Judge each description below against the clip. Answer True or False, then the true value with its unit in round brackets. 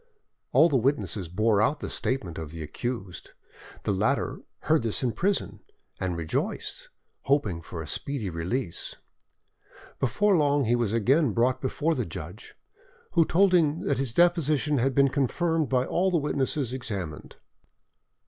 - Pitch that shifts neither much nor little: False (6.6 semitones)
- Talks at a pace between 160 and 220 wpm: False (150 wpm)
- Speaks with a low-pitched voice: True (130 Hz)